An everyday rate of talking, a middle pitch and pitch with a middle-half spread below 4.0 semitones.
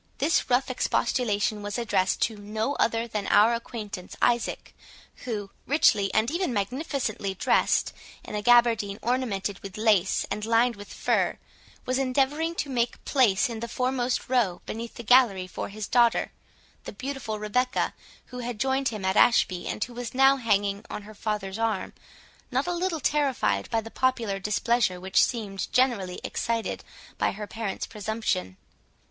No: average, 160 wpm; high, 230 Hz; average, 3.6 semitones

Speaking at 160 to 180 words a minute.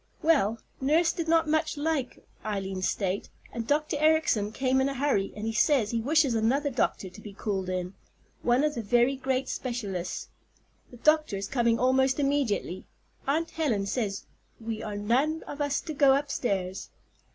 Yes: average, 170 wpm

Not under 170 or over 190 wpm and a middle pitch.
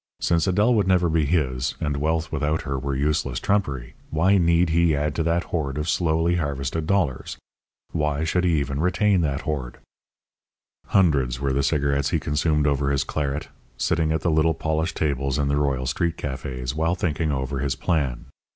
No: average, 180 wpm; very low, 75 Hz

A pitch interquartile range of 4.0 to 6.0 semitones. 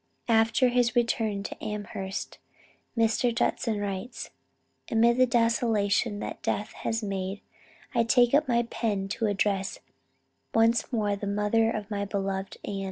No: narrow, 2.6 semitones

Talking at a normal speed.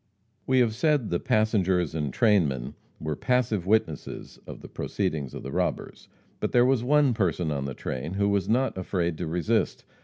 Yes: average, 180 wpm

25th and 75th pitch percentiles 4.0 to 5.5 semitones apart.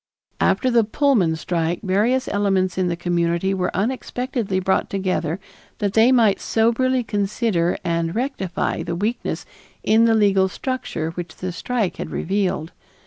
Yes: average, 4.7 semitones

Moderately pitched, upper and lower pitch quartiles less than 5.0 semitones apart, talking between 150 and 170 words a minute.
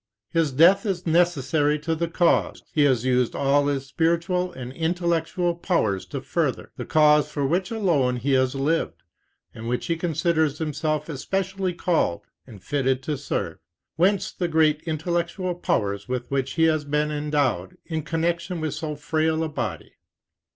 Yes: medium, 155 Hz; average, 3.8 semitones; average, 160 wpm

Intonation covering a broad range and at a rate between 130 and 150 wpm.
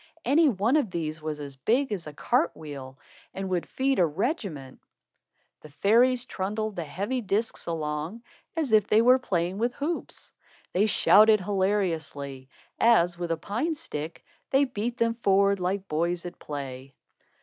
No: wide, 6.7 semitones; average, 160 wpm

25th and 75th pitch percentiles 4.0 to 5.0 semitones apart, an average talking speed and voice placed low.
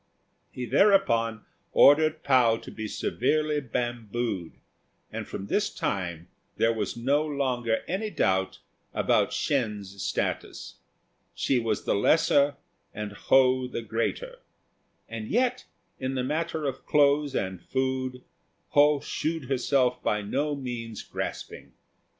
No: average, 4.5 semitones; slow, 120 wpm; low, 130 Hz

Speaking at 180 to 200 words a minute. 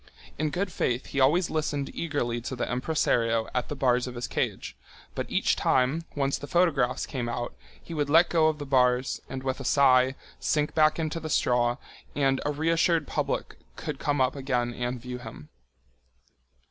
Yes: average, 185 wpm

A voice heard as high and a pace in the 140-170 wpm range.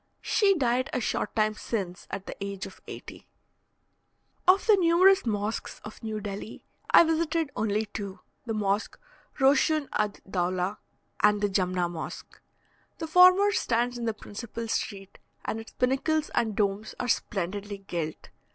Yes: high, 220 Hz; average, 150 wpm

